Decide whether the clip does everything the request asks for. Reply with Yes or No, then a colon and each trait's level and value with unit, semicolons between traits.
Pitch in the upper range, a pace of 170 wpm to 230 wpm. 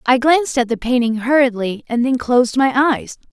Yes: very high, 250 Hz; average, 200 wpm